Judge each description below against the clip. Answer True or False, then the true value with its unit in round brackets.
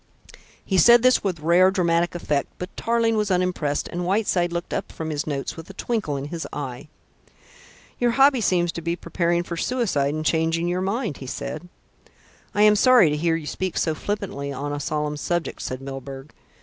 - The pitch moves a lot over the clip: False (4.6 semitones)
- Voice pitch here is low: False (170 Hz)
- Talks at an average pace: True (190 wpm)